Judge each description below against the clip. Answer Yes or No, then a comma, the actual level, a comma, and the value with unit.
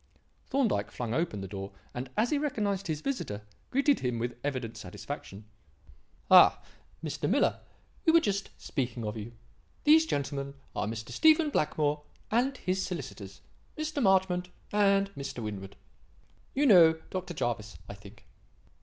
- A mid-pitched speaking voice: Yes, medium, 155 Hz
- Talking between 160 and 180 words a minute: No, average, 145 wpm